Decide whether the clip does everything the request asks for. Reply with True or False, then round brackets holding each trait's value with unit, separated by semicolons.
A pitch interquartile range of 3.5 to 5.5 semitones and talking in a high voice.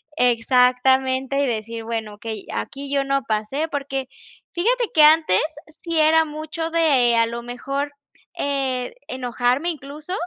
True (3.9 semitones; 270 Hz)